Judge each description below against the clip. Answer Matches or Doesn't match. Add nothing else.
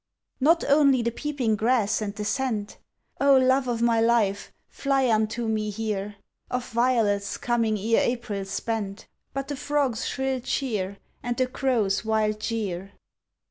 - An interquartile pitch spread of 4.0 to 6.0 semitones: Doesn't match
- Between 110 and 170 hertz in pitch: Doesn't match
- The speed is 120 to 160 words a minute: Matches